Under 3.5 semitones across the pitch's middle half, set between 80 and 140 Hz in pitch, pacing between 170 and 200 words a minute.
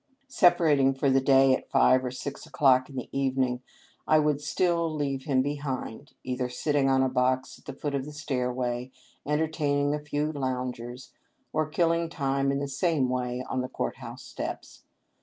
Yes: narrow, 2.5 semitones; low, 135 Hz; average, 185 wpm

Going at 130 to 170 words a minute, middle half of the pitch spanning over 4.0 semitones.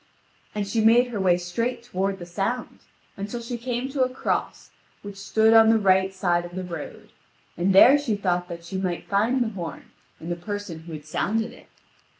No: average, 200 wpm; average, 4.5 semitones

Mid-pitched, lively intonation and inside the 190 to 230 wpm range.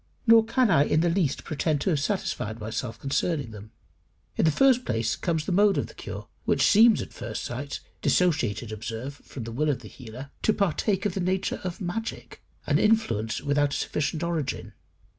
Yes: medium, 150 Hz; wide, 7.6 semitones; average, 195 wpm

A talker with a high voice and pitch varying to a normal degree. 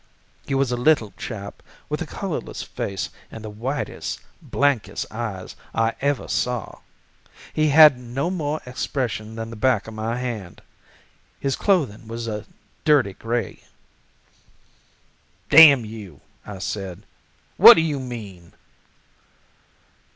No: low, 120 Hz; average, 4.4 semitones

